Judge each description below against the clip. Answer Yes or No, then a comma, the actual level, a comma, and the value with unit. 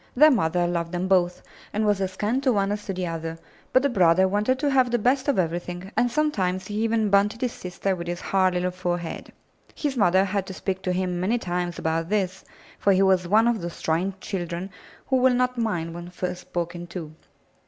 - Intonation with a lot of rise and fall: No, average, 3.8 semitones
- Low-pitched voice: No, high, 190 Hz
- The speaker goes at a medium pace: No, fast, 215 wpm